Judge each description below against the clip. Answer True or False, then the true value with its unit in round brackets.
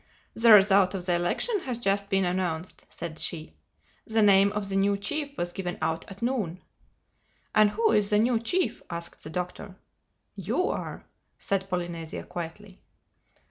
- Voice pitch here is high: True (195 Hz)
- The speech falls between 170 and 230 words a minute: False (160 wpm)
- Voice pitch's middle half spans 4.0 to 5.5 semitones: False (3.3 semitones)